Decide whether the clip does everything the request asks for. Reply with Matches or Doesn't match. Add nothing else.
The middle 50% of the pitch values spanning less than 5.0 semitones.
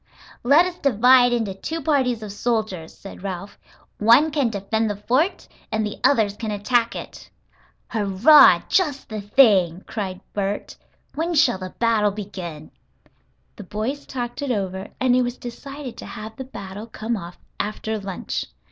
Matches